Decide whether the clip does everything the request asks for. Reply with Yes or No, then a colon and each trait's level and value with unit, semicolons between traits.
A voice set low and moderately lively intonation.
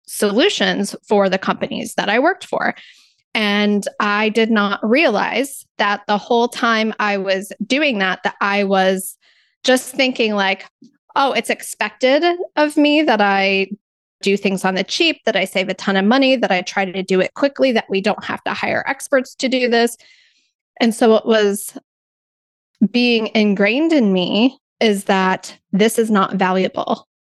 No: high, 215 Hz; average, 4.7 semitones